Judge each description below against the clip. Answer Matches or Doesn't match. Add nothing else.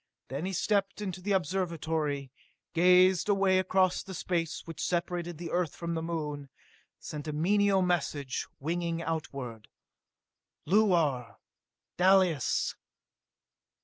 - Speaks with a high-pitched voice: Doesn't match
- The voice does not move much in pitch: Doesn't match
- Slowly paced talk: Matches